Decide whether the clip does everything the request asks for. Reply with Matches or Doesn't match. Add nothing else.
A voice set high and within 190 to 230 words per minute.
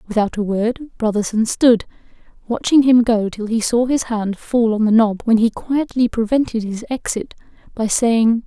Doesn't match